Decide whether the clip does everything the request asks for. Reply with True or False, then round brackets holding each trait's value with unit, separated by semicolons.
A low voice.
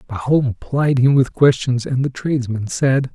True (130 Hz)